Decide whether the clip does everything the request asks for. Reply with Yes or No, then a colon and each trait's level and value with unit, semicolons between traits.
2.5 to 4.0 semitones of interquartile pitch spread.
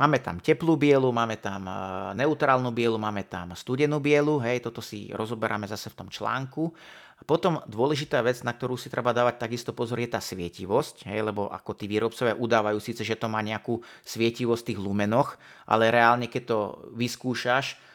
Yes: average, 2.9 semitones